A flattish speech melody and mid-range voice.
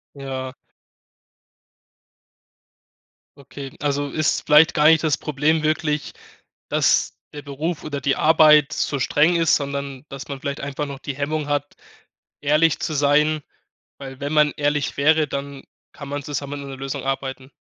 Yes: narrow, 1.6 semitones; medium, 145 Hz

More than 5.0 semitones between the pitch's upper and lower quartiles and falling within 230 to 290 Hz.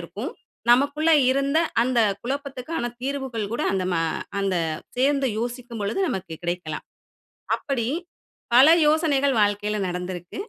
Yes: wide, 5.6 semitones; high, 245 Hz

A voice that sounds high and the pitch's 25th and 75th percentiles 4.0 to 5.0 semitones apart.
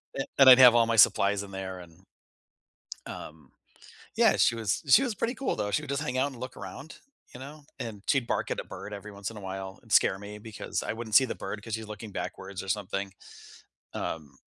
No: low, 105 Hz; average, 4.5 semitones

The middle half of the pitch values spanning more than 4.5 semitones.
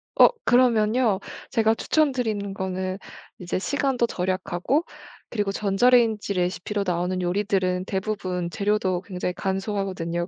No: average, 3.2 semitones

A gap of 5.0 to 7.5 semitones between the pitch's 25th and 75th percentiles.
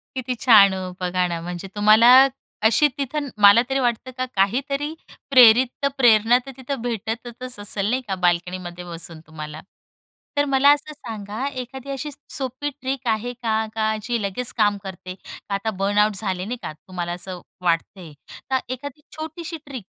Yes: wide, 5.4 semitones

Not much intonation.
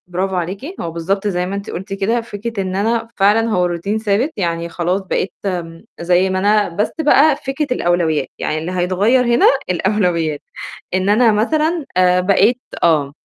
No: average, 3.7 semitones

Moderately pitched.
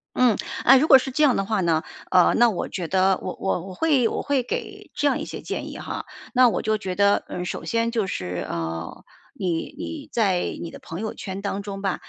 No: high, 200 Hz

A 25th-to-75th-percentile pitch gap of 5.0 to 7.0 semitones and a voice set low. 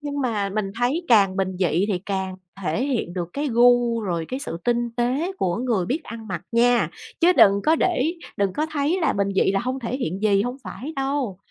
No: wide, 5.5 semitones; high, 235 Hz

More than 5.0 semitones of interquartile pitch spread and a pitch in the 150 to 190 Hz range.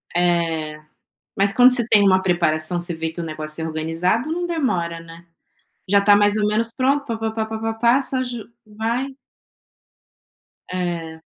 No: wide, 5.6 semitones; high, 200 Hz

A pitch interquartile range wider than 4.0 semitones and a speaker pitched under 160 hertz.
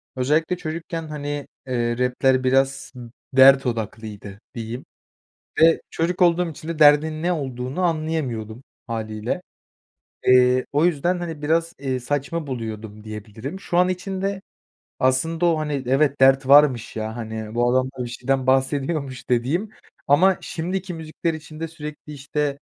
Yes: average, 4.5 semitones; medium, 140 Hz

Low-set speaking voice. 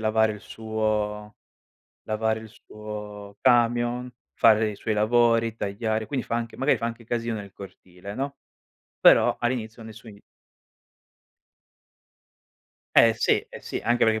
Yes: low, 110 Hz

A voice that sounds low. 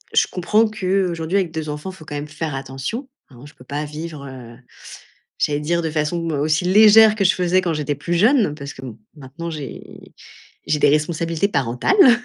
No: medium, 160 Hz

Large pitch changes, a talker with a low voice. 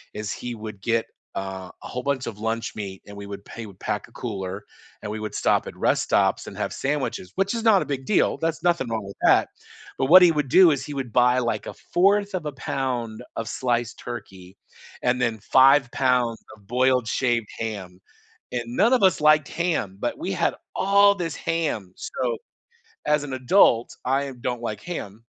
Yes: wide, 5.7 semitones; low, 125 Hz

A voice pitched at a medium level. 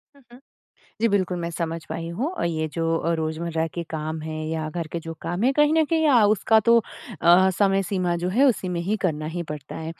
Yes: medium, 175 Hz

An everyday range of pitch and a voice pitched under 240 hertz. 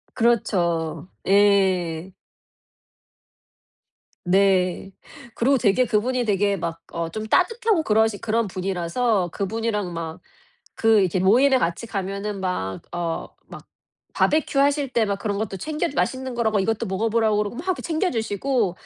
Yes: average, 4.2 semitones; high, 210 Hz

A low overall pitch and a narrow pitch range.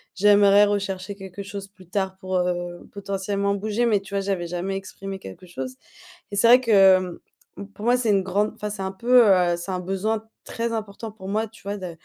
No: high, 195 Hz; narrow, 1.8 semitones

